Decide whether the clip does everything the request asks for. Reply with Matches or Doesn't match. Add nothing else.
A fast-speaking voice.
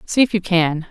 Matches